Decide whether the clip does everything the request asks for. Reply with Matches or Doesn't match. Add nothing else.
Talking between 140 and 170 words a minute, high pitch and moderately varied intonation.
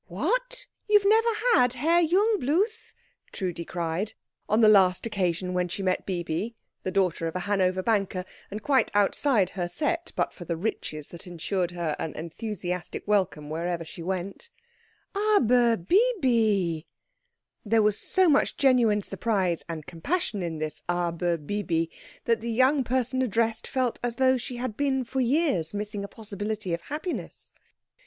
Doesn't match